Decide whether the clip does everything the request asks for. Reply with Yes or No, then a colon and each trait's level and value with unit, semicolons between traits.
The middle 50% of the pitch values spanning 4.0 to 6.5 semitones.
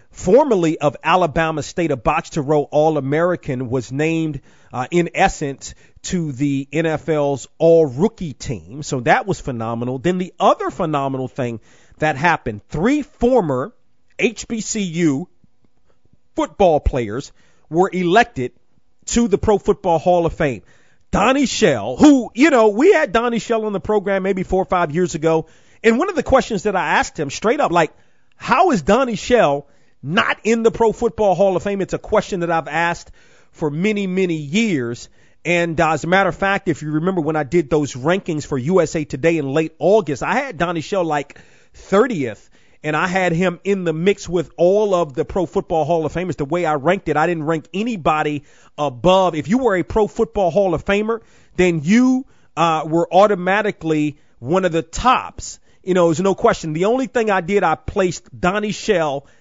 Yes: average, 4.6 semitones